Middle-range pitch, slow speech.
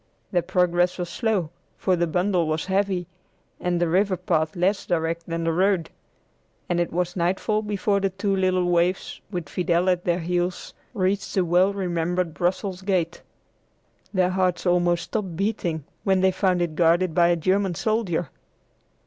No: medium, 180 Hz; average, 165 wpm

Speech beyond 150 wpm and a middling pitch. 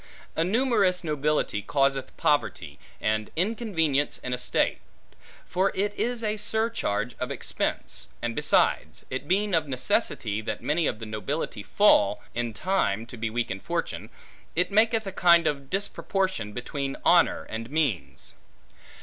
No: average, 145 wpm; medium, 145 Hz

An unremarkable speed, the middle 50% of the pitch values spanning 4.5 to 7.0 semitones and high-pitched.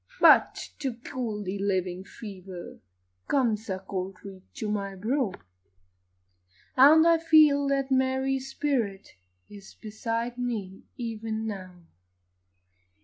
No: slow, 110 wpm; average, 5.2 semitones; high, 220 Hz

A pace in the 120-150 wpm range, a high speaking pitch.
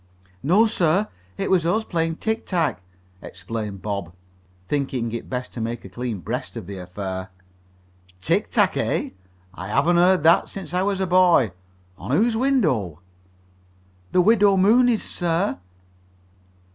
No: average, 145 wpm; medium, 160 Hz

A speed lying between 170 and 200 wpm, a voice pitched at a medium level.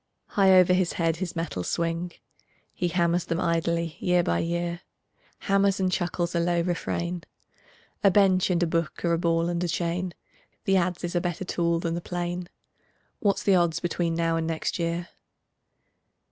Yes: average, 175 wpm; medium, 175 Hz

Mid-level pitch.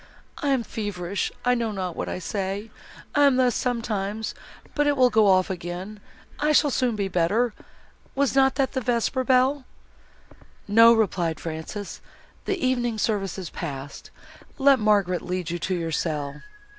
No: high, 215 Hz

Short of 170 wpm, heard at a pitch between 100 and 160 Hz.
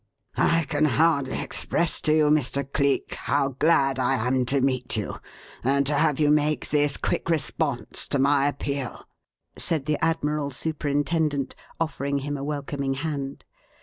Yes: average, 150 wpm; medium, 140 Hz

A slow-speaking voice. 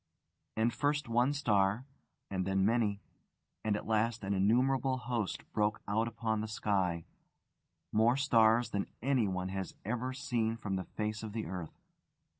No: average, 150 wpm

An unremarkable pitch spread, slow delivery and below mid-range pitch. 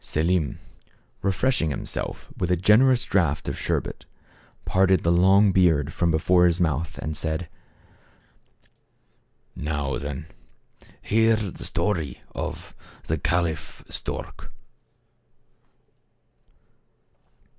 Yes: average, 3.5 semitones; slow, 95 wpm; very low, 85 Hz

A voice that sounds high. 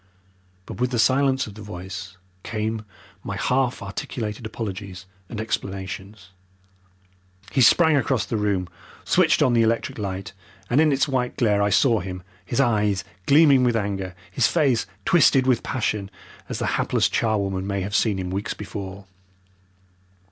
No: low, 110 Hz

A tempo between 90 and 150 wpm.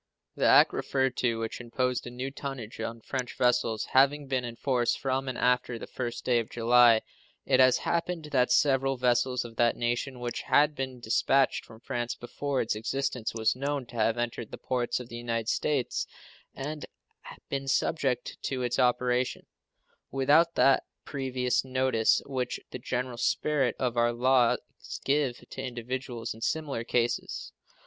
No: average, 160 wpm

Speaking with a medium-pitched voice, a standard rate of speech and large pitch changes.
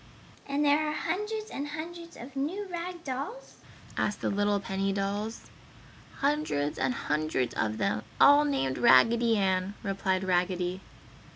No: high, 220 Hz; average, 145 wpm; wide, 8.2 semitones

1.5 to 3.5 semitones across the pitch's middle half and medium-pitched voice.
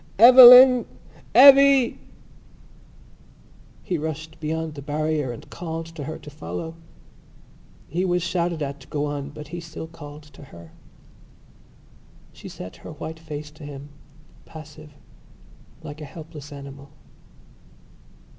Yes: narrow, 2.5 semitones; medium, 155 Hz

